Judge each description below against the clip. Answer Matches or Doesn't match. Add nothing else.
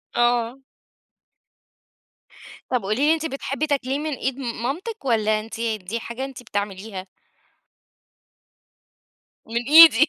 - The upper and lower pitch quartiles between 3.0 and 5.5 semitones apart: Matches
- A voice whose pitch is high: Matches